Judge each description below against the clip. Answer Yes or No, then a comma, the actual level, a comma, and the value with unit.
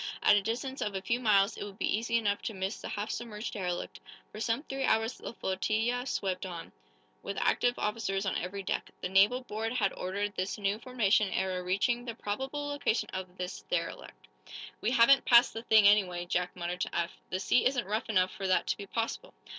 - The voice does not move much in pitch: No, average, 3.7 semitones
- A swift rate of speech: Yes, fast, 210 wpm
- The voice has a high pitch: Yes, high, 210 Hz